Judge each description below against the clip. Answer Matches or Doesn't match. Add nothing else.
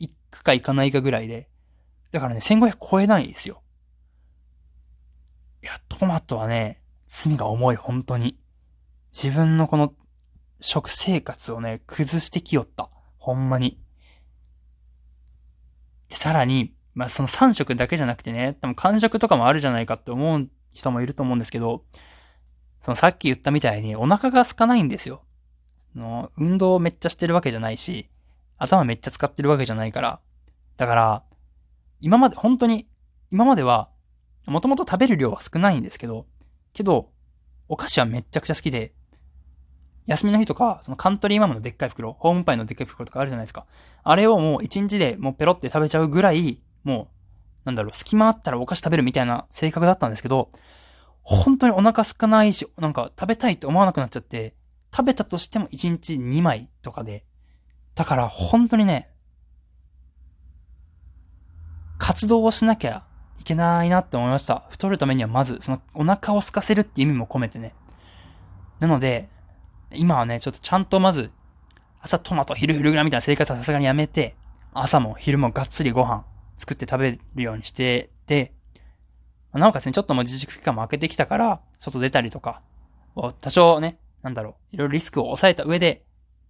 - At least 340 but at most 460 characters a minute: Matches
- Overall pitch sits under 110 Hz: Doesn't match